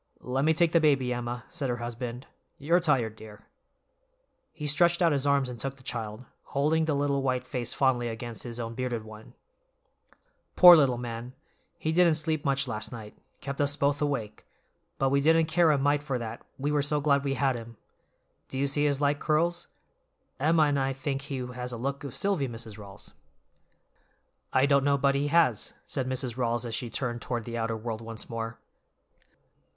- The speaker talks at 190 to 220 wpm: Yes, average, 195 wpm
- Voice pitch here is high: No, low, 135 Hz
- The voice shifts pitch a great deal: No, average, 3.5 semitones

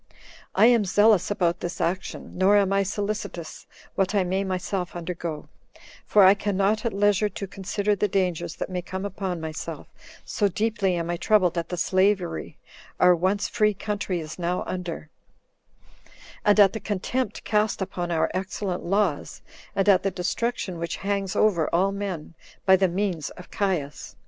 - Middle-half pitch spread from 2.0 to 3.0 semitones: Yes, narrow, 2.6 semitones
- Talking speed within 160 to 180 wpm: Yes, average, 170 wpm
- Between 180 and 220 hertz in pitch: Yes, high, 190 Hz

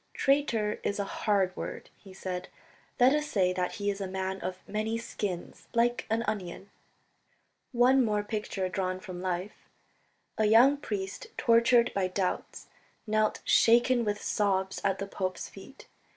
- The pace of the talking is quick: No, average, 155 wpm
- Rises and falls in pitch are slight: No, average, 3.5 semitones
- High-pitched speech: Yes, high, 205 Hz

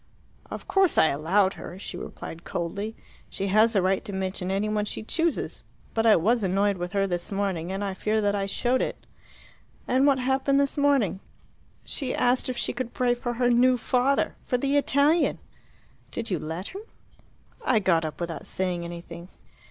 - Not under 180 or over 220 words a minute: Yes, average, 185 wpm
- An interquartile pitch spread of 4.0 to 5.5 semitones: Yes, average, 5.2 semitones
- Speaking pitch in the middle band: No, high, 210 Hz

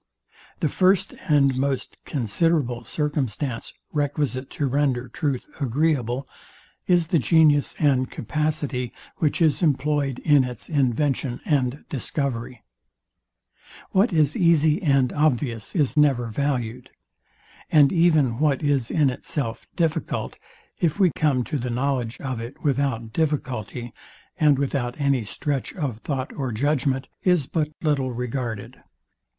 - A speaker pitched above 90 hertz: Yes, medium, 140 Hz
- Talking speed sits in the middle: No, slow, 125 wpm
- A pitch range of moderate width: Yes, average, 3.3 semitones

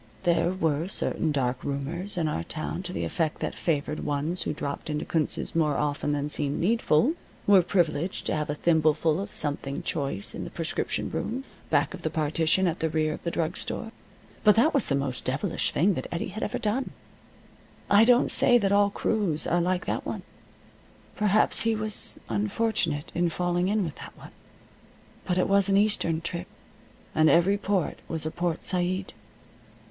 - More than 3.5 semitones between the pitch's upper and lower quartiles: Yes, average, 4.7 semitones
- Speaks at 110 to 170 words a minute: No, average, 185 wpm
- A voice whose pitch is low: No, medium, 170 Hz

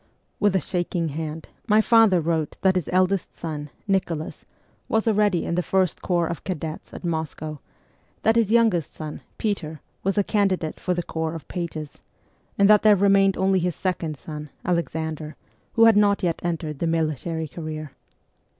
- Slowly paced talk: No, average, 170 wpm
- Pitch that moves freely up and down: No, average, 3.7 semitones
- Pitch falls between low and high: Yes, medium, 175 Hz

